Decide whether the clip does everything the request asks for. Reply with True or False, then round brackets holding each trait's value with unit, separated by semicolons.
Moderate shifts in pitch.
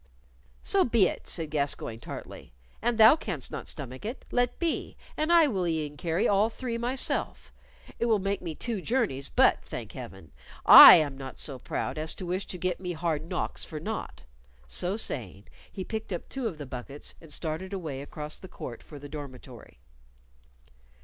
False (7.2 semitones)